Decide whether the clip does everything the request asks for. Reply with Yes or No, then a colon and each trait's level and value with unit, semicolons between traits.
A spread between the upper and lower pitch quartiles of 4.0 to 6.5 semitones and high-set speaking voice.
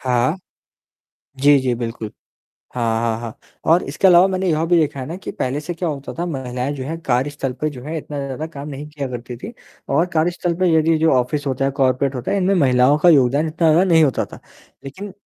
No: average, 4.3 semitones; medium, 145 Hz